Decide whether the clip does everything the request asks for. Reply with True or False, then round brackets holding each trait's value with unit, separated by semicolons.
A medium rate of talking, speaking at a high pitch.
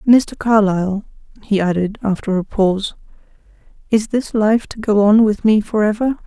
True (155 wpm; 210 Hz)